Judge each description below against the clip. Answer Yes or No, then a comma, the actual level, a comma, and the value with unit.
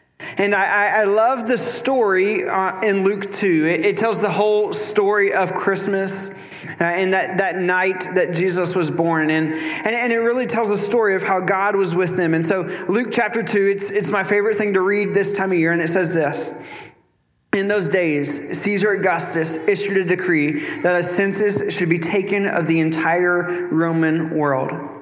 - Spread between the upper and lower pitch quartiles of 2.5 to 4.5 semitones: Yes, average, 2.9 semitones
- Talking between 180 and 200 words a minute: Yes, average, 190 wpm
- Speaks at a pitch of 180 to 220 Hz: Yes, high, 190 Hz